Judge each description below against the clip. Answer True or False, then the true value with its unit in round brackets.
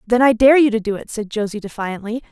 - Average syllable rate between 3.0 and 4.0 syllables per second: False (6.1 syllables/s)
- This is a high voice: True (225 Hz)